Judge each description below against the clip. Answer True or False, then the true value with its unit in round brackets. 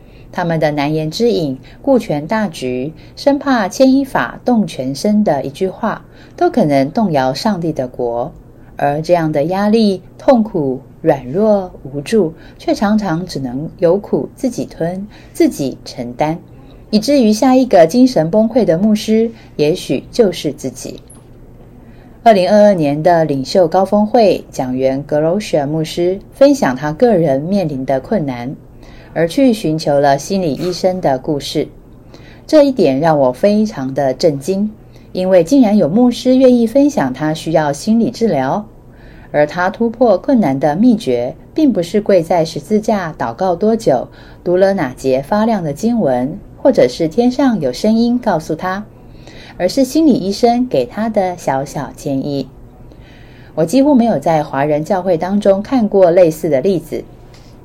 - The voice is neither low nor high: True (180 Hz)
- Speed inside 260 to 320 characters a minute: False (225 characters per minute)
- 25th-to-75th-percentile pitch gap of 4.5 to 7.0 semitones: False (7.6 semitones)